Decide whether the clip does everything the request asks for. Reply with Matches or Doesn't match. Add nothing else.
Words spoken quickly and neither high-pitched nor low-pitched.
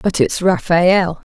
Doesn't match